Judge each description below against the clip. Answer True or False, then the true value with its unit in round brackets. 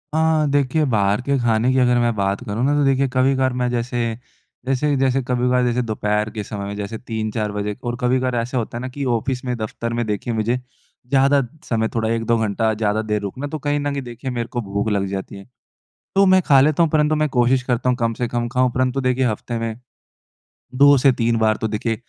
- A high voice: False (120 Hz)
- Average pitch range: True (3.1 semitones)